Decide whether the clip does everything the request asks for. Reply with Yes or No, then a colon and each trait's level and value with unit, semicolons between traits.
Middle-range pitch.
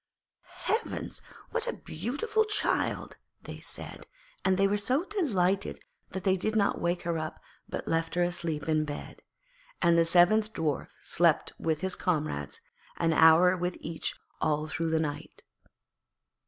Yes: medium, 175 Hz